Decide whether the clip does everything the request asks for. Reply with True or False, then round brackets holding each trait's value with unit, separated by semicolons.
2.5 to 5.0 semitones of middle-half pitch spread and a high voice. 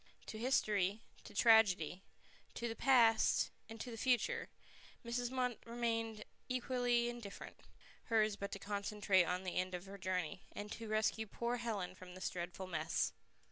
True (4.0 semitones; 215 Hz)